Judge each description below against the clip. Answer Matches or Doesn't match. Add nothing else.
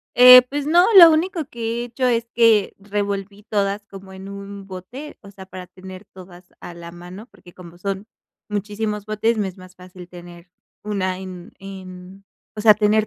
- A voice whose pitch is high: Matches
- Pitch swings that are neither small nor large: Matches